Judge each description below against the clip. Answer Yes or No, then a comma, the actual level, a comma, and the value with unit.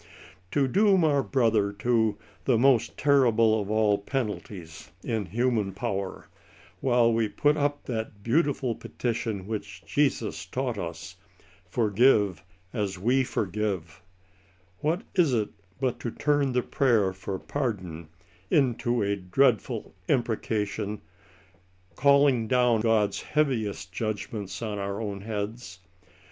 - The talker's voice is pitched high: No, low, 110 Hz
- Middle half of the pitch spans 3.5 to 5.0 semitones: Yes, average, 4.0 semitones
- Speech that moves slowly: Yes, slow, 130 wpm